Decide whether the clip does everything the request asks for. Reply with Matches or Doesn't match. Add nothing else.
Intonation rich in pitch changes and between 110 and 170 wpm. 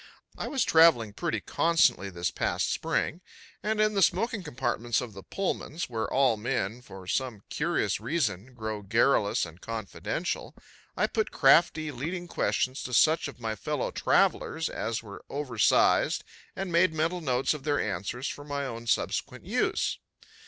Matches